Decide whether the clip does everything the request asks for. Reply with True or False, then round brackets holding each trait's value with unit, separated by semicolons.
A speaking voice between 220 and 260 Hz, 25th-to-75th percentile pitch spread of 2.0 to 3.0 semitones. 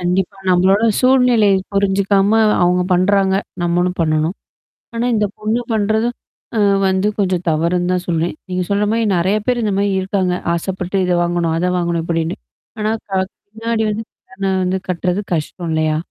False (190 Hz; 2.7 semitones)